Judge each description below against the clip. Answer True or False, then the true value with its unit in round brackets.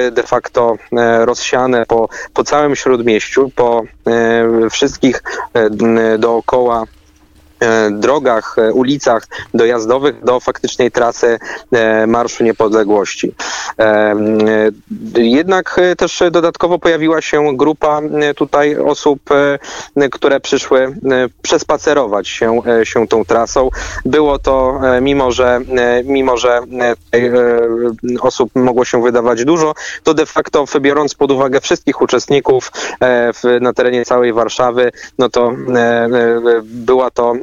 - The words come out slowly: True (105 wpm)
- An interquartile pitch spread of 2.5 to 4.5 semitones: True (3.3 semitones)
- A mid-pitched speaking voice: False (125 Hz)